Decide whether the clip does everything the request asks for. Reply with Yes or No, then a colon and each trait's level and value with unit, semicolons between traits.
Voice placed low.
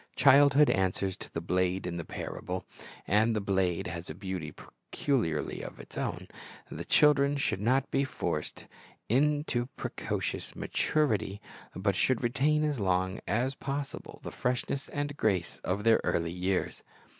Yes: low, 110 Hz